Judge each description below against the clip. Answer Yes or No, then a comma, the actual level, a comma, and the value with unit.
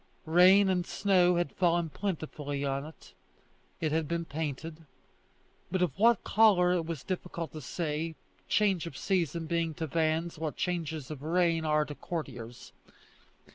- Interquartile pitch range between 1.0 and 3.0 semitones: Yes, average, 2.7 semitones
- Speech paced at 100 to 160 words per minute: Yes, average, 150 wpm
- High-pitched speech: No, medium, 165 Hz